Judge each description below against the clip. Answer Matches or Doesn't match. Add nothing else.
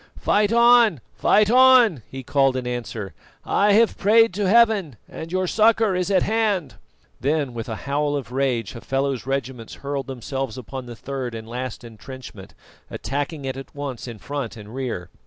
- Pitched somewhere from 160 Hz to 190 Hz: Doesn't match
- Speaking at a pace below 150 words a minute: Doesn't match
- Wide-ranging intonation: Matches